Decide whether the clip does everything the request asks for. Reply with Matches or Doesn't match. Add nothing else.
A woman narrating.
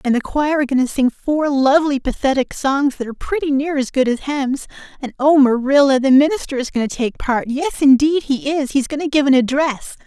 Matches